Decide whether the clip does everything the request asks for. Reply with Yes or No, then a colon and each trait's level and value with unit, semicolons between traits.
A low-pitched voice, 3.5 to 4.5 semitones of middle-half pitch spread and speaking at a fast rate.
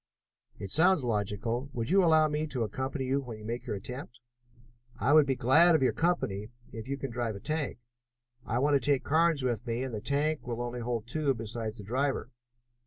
Yes: low, 130 Hz; average, 4.2 semitones; fast, 210 wpm